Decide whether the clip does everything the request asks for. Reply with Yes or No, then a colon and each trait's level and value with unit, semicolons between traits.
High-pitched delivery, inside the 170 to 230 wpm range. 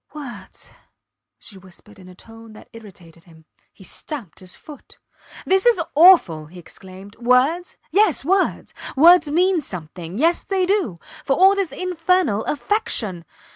No: very high, 250 Hz; average, 140 wpm